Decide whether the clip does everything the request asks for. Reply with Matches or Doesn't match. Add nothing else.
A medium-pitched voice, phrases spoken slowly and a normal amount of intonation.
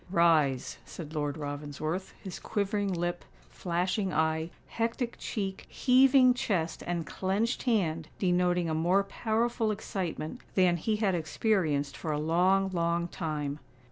Matches